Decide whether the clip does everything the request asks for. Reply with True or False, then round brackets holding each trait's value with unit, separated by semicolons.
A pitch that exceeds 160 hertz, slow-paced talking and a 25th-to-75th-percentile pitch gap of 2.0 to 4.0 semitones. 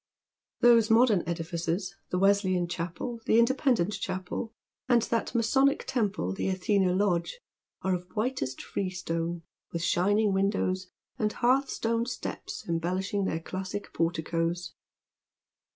False (190 Hz; 115 wpm; 4.5 semitones)